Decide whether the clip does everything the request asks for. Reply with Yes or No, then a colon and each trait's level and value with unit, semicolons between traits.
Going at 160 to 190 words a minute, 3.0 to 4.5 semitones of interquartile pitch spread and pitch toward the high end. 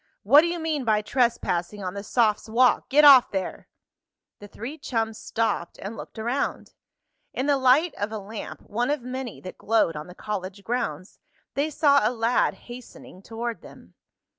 Yes: average, 175 wpm; average, 4.2 semitones; high, 230 Hz